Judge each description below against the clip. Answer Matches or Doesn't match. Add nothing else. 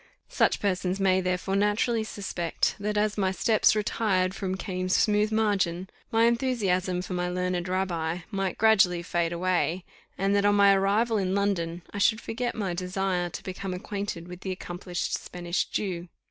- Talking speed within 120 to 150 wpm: Doesn't match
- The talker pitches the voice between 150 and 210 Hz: Matches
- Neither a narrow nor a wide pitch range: Doesn't match